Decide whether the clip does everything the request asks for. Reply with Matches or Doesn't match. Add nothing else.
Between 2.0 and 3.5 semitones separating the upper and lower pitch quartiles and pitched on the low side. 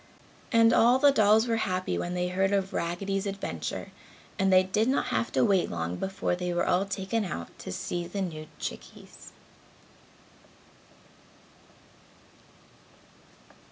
Doesn't match